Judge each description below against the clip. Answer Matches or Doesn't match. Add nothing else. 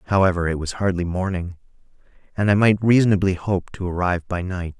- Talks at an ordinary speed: Matches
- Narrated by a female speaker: Doesn't match